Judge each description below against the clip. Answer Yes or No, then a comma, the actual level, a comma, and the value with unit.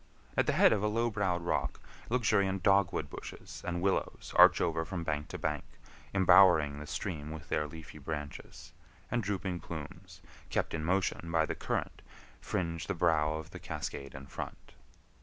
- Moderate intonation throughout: Yes, average, 4.0 semitones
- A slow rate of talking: No, average, 170 wpm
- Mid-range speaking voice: No, very low, 85 Hz